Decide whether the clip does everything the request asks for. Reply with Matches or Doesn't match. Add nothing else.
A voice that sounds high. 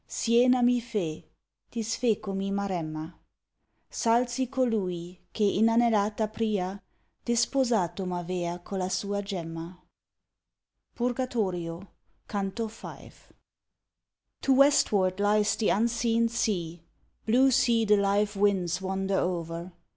Matches